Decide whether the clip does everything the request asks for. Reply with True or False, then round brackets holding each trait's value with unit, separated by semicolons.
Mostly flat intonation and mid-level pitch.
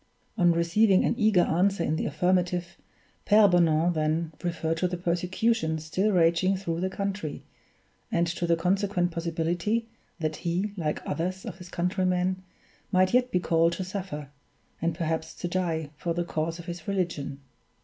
True (2.2 semitones; 175 Hz)